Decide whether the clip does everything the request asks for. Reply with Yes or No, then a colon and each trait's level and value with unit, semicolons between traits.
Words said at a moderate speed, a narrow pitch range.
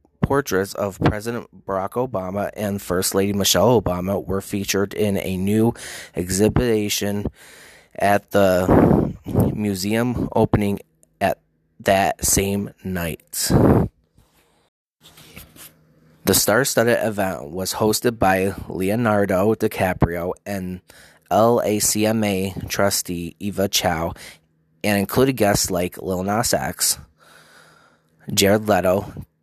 No: slow, 95 wpm; narrow, 2.3 semitones